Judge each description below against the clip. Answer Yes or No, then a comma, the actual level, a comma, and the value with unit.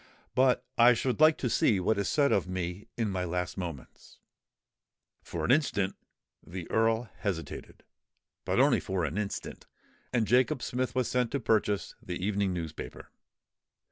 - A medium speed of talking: Yes, average, 150 wpm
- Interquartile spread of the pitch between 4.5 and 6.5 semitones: Yes, average, 5.1 semitones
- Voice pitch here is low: Yes, low, 105 Hz